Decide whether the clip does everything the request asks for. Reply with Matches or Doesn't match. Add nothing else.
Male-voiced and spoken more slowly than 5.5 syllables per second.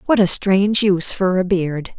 Doesn't match